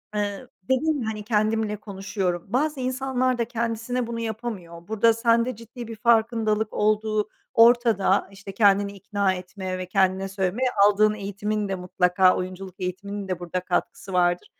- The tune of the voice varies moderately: Yes, average, 3.3 semitones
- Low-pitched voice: No, high, 210 Hz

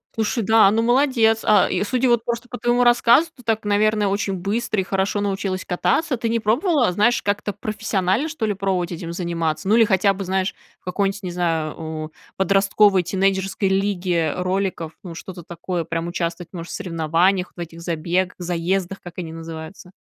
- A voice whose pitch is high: Yes, high, 195 Hz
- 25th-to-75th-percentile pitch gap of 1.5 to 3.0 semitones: No, average, 3.6 semitones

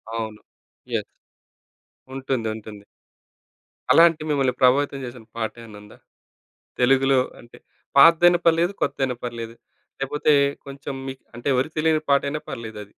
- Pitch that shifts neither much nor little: Yes, average, 4.1 semitones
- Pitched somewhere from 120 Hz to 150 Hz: Yes, low, 135 Hz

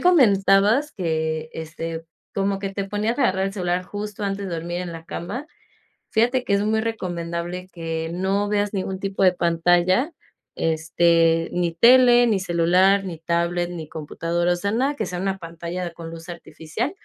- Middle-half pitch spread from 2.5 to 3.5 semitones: Yes, average, 3.2 semitones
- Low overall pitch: No, medium, 180 Hz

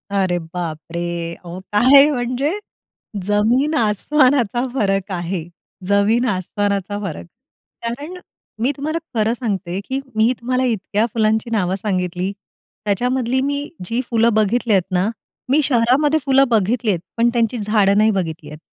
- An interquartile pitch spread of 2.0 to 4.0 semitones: No, average, 4.7 semitones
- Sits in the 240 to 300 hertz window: No, high, 215 Hz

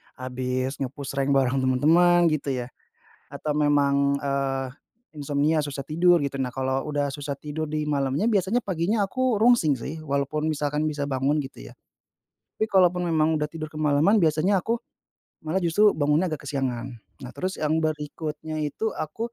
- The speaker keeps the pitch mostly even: No, average, 3.1 semitones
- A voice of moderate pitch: Yes, medium, 150 Hz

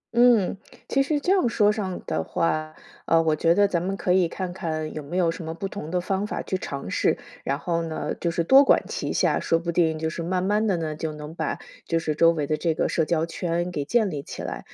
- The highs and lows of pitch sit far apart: No, average, 3.2 semitones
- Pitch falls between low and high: Yes, medium, 170 Hz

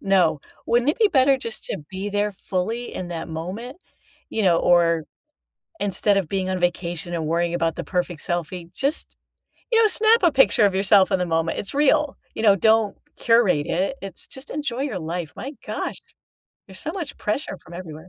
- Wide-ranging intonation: Yes, wide, 5.7 semitones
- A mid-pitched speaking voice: No, high, 195 Hz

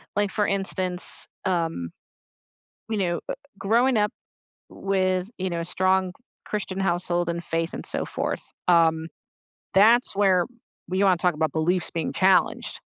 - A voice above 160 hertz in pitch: Yes, medium, 185 Hz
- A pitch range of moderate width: No, narrow, 2.3 semitones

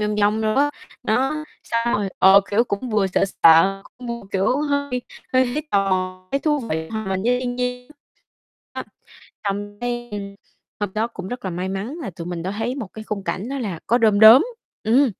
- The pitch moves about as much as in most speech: Yes, average, 4.2 semitones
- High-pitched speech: Yes, high, 215 Hz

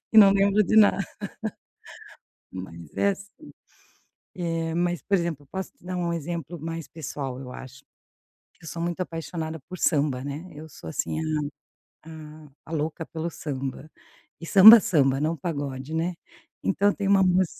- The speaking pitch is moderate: Yes, medium, 165 Hz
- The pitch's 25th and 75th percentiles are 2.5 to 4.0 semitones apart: Yes, average, 3.7 semitones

